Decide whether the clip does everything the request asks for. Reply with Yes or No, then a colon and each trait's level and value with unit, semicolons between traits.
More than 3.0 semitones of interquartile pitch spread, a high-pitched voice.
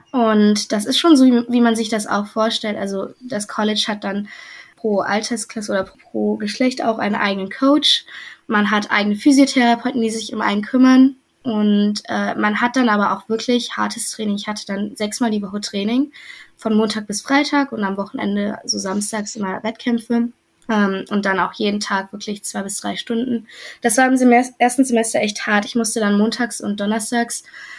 No: average, 2.7 semitones; high, 220 Hz